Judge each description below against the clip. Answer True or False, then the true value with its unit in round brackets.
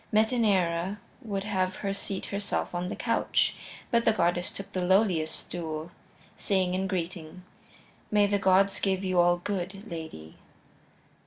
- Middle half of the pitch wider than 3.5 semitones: False (2.4 semitones)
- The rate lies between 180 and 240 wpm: False (145 wpm)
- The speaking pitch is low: False (185 Hz)